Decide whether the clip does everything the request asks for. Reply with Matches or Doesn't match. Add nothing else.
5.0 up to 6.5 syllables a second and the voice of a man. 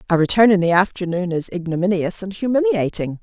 Doesn't match